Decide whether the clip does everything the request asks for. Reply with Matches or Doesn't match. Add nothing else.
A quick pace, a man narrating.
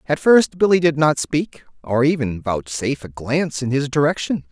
Doesn't match